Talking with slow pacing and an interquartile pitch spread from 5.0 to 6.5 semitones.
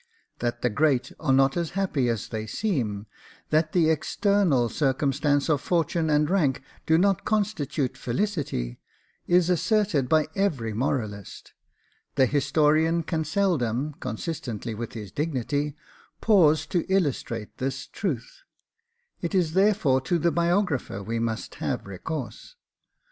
Yes: slow, 130 wpm; wide, 5.6 semitones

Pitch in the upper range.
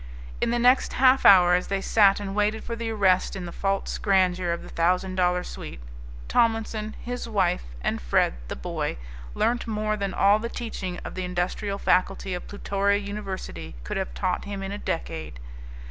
Yes: high, 195 Hz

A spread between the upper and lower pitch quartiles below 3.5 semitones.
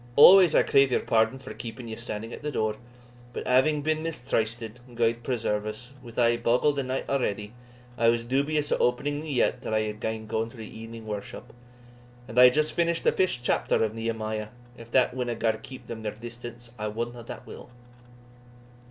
Yes: average, 2.8 semitones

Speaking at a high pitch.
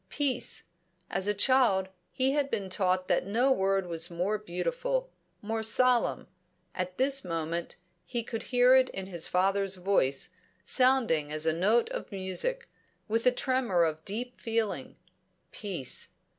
Yes: high, 205 Hz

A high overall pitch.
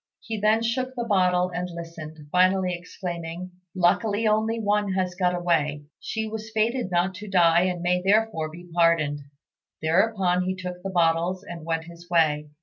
No: medium, 180 Hz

